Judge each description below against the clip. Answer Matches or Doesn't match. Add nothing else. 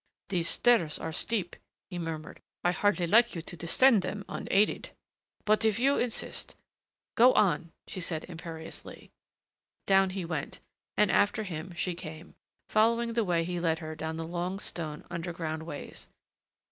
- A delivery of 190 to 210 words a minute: Doesn't match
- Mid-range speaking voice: Matches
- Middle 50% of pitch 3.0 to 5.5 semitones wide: Matches